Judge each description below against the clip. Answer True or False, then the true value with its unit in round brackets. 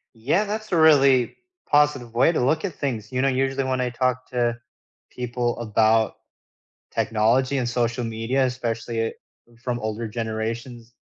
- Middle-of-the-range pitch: False (125 Hz)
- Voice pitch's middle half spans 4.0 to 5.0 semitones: False (2.7 semitones)